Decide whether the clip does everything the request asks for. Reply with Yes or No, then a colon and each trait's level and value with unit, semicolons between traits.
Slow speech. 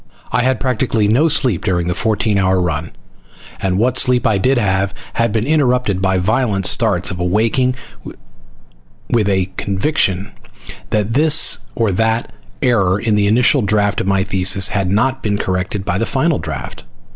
No: average, 165 wpm